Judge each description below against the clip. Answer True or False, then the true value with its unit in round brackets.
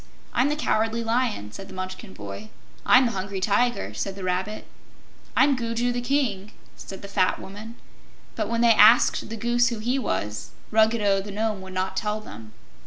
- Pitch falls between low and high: False (215 Hz)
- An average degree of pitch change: True (3.6 semitones)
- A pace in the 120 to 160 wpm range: False (180 wpm)